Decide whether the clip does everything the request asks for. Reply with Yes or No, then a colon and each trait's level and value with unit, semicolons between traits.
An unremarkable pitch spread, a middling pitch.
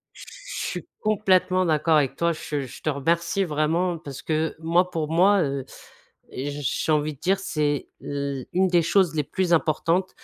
Yes: average, 3.7 semitones; medium, 160 Hz